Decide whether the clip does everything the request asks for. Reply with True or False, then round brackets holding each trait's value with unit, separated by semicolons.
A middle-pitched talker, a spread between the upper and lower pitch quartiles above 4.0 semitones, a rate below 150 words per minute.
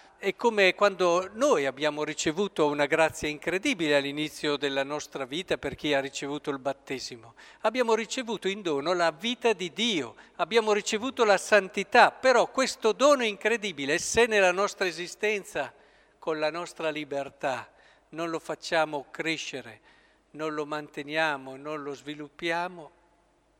True (165 Hz; 5.5 semitones; 135 wpm)